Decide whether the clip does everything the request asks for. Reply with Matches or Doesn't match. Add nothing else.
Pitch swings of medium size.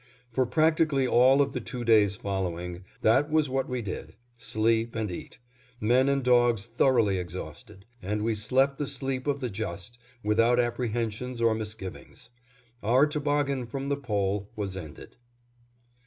Matches